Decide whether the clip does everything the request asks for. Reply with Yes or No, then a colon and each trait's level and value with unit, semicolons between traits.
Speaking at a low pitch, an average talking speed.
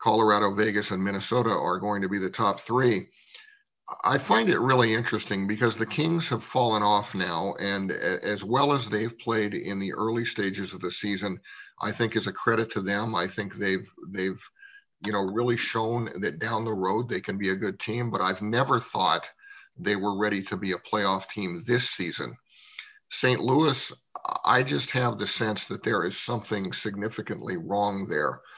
Yes: low, 105 Hz; average, 185 wpm